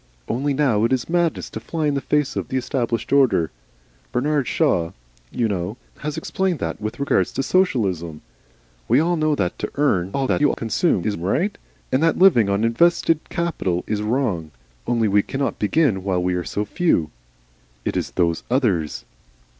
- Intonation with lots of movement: Yes, wide, 7.1 semitones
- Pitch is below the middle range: Yes, low, 120 Hz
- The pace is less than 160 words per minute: No, average, 175 wpm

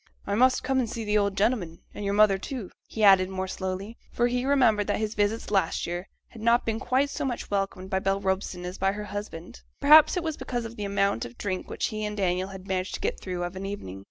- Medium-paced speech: No, fast, 245 wpm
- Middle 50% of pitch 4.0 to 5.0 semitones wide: No, average, 3.3 semitones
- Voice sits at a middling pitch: No, high, 205 Hz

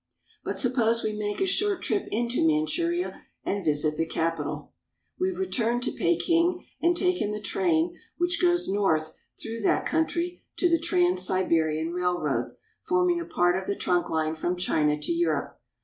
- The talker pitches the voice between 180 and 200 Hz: No, high, 210 Hz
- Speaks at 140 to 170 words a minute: Yes, average, 165 wpm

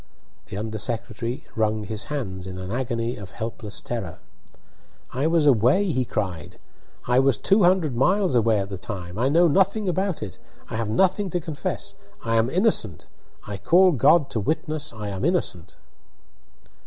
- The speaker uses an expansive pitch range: Yes, wide, 7.4 semitones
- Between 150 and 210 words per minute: Yes, average, 165 wpm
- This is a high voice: No, low, 120 Hz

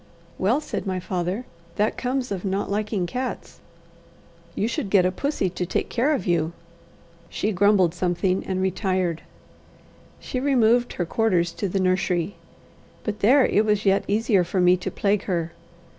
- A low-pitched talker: No, high, 195 Hz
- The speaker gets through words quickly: No, average, 160 wpm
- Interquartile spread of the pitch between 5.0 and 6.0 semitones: No, average, 3.3 semitones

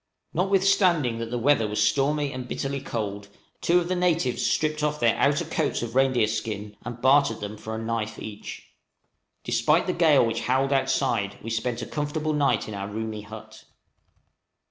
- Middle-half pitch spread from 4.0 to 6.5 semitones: Yes, average, 5.2 semitones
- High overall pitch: No, low, 130 Hz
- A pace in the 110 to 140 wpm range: No, average, 180 wpm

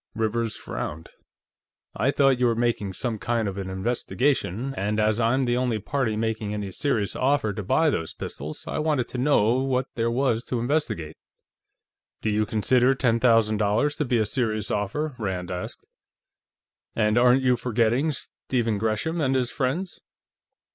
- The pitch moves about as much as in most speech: Yes, average, 3.5 semitones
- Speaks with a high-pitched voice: No, low, 115 Hz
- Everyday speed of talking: Yes, average, 165 wpm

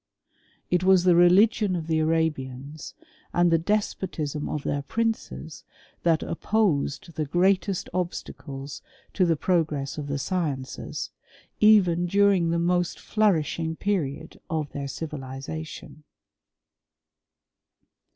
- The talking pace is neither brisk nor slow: No, slow, 105 wpm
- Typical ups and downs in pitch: Yes, average, 3.7 semitones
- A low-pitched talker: No, medium, 165 Hz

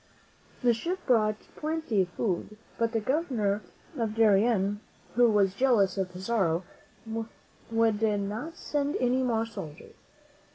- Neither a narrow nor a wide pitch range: Yes, average, 3.6 semitones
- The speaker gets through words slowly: Yes, slow, 125 wpm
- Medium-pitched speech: No, high, 225 Hz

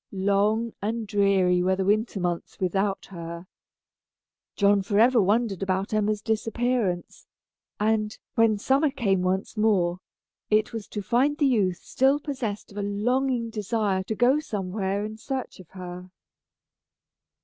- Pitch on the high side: Yes, high, 210 Hz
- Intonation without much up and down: No, average, 3.2 semitones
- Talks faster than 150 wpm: No, average, 140 wpm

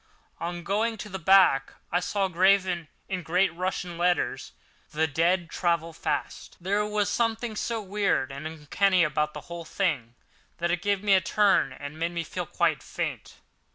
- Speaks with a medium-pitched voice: Yes, medium, 180 Hz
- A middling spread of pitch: Yes, average, 3.3 semitones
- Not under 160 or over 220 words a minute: Yes, average, 170 wpm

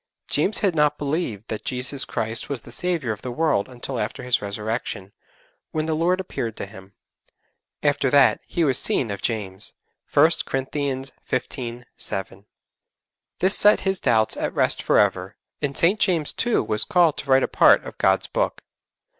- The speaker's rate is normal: Yes, average, 170 wpm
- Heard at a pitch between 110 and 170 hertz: Yes, low, 135 Hz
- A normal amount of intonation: No, wide, 6.0 semitones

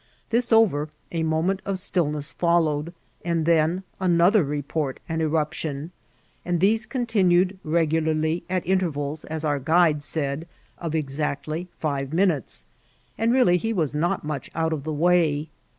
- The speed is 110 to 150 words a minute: Yes, average, 140 wpm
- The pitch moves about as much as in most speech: Yes, average, 3.0 semitones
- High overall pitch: No, medium, 160 Hz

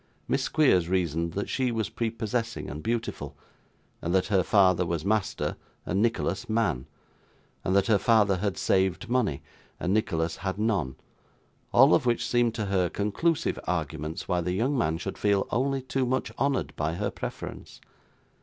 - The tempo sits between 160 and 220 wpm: Yes, average, 165 wpm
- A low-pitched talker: Yes, low, 100 Hz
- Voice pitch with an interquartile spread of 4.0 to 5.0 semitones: Yes, average, 4.6 semitones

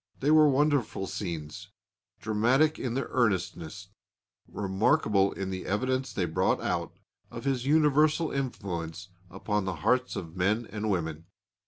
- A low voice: Yes, low, 105 Hz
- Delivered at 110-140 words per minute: Yes, slow, 135 wpm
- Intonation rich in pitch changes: Yes, wide, 6.1 semitones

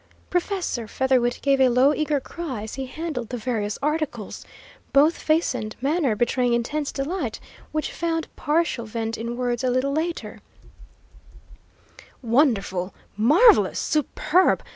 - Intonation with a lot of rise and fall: No, average, 4.6 semitones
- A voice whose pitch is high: Yes, very high, 265 Hz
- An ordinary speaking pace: No, slow, 130 wpm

